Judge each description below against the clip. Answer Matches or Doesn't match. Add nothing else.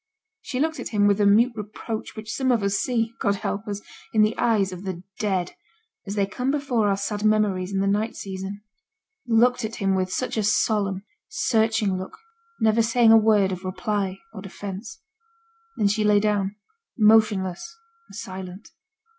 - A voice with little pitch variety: Matches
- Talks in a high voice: Matches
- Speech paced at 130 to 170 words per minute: Doesn't match